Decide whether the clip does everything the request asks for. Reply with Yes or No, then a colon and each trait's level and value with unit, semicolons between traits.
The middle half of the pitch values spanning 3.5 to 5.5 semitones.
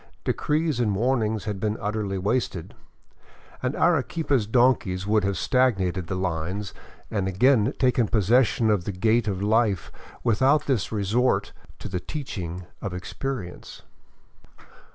Yes: average, 4.8 semitones